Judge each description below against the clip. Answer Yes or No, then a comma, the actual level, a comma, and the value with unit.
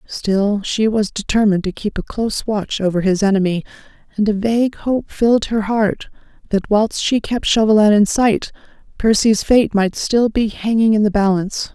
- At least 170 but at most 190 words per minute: Yes, average, 180 wpm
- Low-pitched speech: No, high, 210 Hz